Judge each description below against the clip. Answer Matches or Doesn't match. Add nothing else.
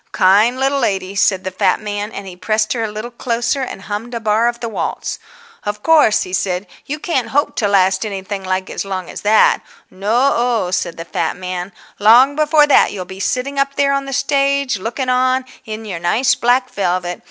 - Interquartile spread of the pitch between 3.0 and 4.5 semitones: Doesn't match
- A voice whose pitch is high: Matches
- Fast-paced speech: Matches